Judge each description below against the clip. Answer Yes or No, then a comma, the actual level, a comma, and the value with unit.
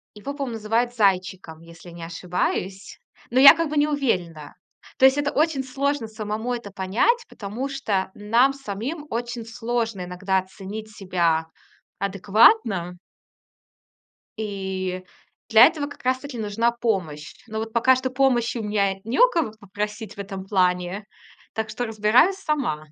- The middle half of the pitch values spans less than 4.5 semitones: No, average, 5.1 semitones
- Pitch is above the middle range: Yes, high, 220 Hz